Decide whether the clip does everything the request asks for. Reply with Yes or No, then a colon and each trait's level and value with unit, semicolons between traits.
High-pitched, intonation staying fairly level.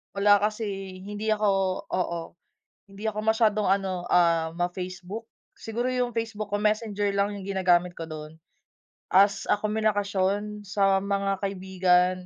Yes: high, 200 Hz; narrow, 2.3 semitones